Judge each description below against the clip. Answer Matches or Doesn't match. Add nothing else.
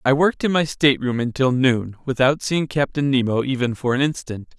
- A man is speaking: Matches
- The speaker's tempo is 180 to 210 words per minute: Matches